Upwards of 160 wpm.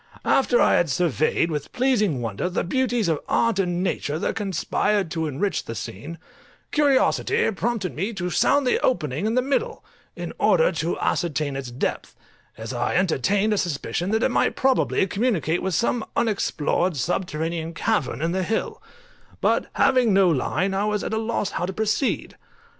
Yes: average, 170 wpm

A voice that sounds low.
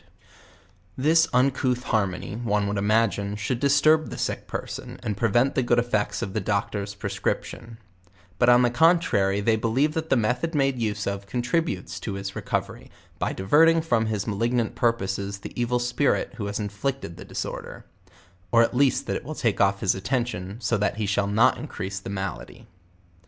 Yes: low, 115 Hz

